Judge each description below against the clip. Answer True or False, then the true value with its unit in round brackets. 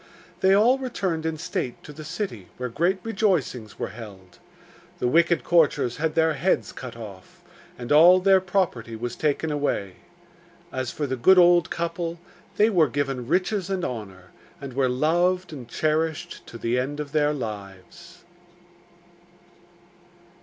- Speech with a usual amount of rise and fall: False (6.3 semitones)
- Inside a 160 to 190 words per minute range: False (150 wpm)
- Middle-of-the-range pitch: True (150 Hz)